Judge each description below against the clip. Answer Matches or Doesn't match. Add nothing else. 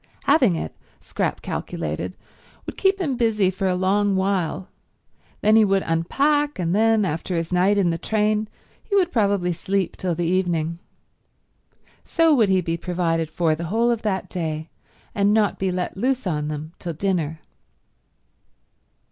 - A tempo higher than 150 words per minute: Matches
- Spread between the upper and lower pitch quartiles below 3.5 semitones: Doesn't match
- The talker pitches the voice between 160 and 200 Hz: Matches